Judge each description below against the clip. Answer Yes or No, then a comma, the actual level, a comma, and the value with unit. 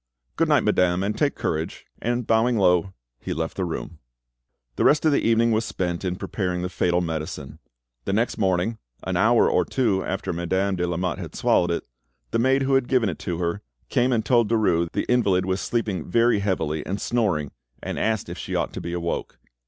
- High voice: No, very low, 95 Hz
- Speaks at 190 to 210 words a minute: Yes, fast, 205 wpm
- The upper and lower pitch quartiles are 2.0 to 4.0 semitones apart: No, average, 4.8 semitones